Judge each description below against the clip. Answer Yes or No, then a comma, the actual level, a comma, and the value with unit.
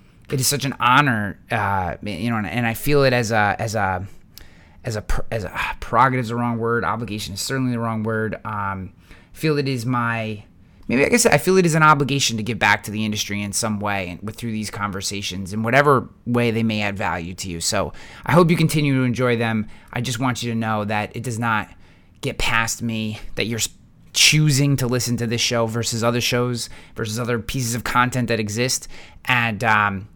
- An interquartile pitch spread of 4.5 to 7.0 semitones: No, average, 3.2 semitones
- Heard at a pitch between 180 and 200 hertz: No, low, 115 Hz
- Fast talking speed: Yes, fast, 220 wpm